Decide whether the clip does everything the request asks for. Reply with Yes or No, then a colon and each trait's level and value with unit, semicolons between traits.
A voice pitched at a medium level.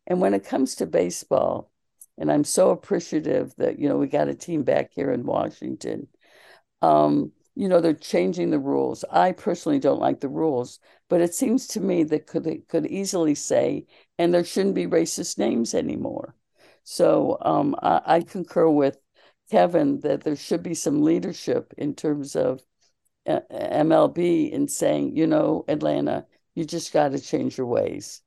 Yes: medium, 165 Hz